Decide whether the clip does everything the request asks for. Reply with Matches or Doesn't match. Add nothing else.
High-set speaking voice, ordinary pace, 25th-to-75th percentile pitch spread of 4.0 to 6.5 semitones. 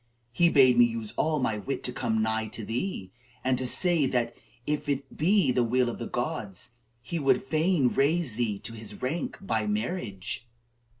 Doesn't match